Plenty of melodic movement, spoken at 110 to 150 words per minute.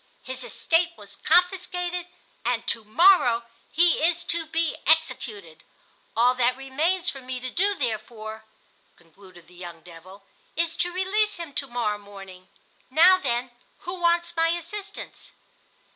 Yes: wide, 8.0 semitones; average, 140 wpm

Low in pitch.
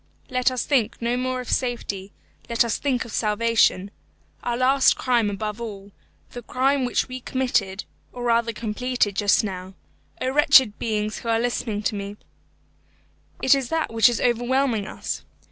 No: high, 235 Hz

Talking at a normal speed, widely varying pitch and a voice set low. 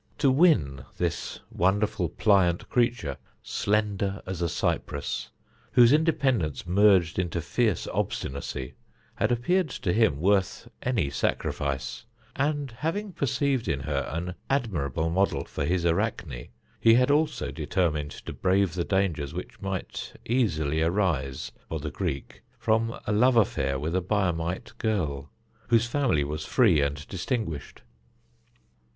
No: slow, 130 wpm; wide, 7.0 semitones; very low, 95 Hz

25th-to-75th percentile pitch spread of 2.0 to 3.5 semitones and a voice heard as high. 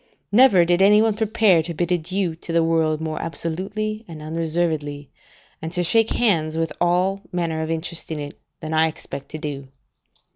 No: average, 3.0 semitones; medium, 165 Hz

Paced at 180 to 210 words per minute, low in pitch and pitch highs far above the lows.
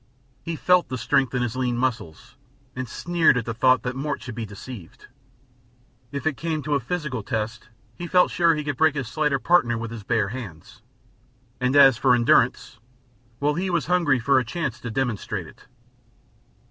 No: average, 185 wpm; low, 130 Hz; average, 4.3 semitones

